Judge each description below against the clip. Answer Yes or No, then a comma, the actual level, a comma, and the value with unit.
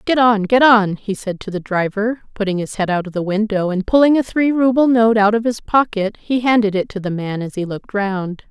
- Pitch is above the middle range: Yes, high, 210 Hz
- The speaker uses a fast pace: Yes, fast, 255 wpm